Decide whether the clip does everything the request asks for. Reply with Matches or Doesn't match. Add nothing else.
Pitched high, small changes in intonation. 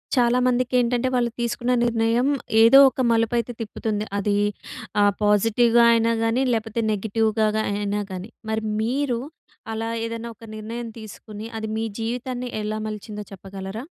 Matches